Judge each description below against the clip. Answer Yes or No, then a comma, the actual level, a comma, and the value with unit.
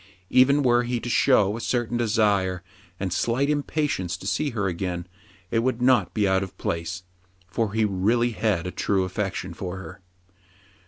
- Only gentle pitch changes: No, average, 4.4 semitones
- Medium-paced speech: Yes, average, 175 wpm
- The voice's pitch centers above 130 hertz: No, low, 105 Hz